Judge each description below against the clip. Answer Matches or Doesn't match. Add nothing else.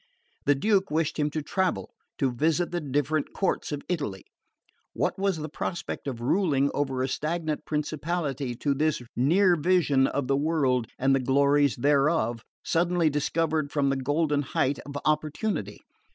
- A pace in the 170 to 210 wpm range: Doesn't match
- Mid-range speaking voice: Matches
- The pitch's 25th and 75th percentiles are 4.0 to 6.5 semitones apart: Doesn't match